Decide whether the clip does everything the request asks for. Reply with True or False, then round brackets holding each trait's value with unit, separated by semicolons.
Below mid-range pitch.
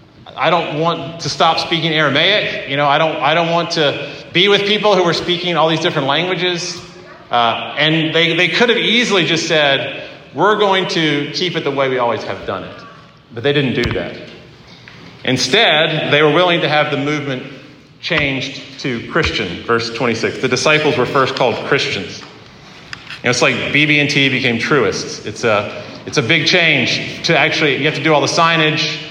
False (155 Hz)